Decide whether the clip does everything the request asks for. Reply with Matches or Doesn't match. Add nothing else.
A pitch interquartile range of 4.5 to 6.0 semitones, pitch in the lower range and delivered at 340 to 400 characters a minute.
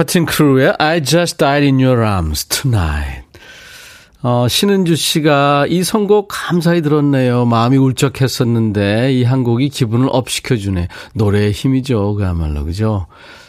Matches